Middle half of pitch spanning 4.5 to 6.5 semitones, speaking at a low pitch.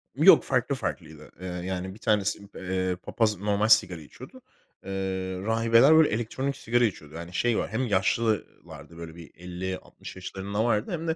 No: average, 4.1 semitones; low, 100 Hz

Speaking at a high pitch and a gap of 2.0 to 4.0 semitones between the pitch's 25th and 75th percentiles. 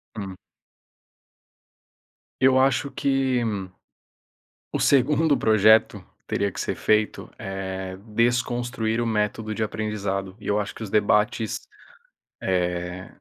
No: low, 110 Hz; average, 3.6 semitones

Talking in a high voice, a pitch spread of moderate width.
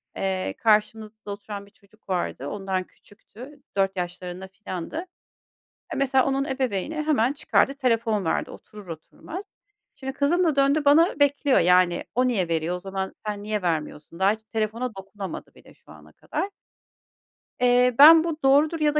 No: high, 220 Hz; wide, 6.3 semitones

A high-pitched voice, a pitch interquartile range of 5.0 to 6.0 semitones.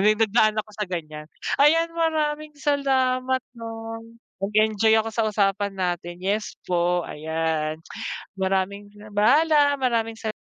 Yes: high, 215 Hz; average, 5.3 semitones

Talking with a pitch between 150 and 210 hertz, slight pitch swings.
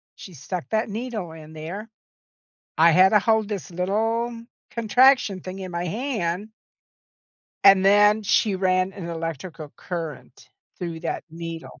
No: medium, 185 Hz; average, 4.3 semitones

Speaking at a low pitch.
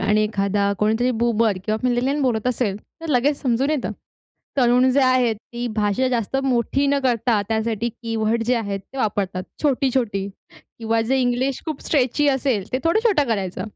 No: high, 240 Hz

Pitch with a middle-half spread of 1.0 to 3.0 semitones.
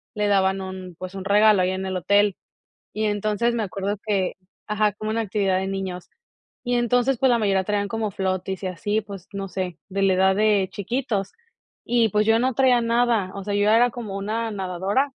Yes: average, 2.7 semitones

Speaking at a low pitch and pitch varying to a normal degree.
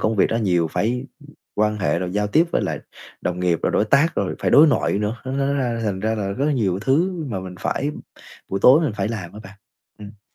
No: low, 105 Hz; wide, 5.7 semitones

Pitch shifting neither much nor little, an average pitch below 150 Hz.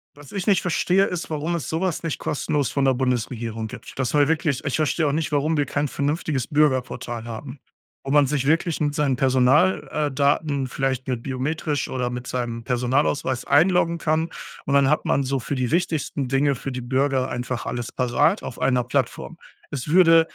Yes: average, 3.3 semitones; medium, 140 Hz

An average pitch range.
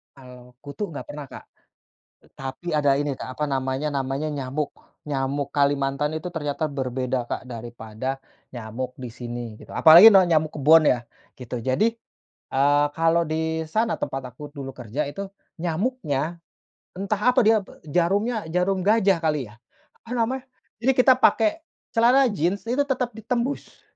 No: wide, 6.8 semitones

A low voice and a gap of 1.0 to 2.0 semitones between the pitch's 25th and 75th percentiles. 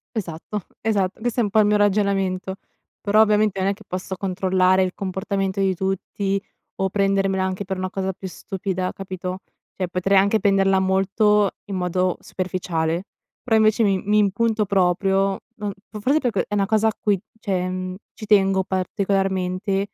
No: high, 195 Hz; narrow, 1.7 semitones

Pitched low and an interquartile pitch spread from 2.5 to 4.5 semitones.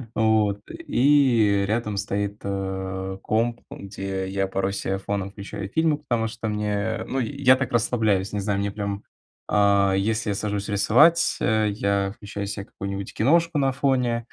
Yes: low, 105 Hz; average, 2.9 semitones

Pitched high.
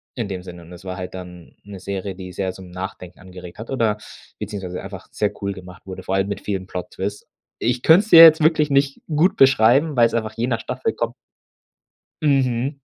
No: low, 100 Hz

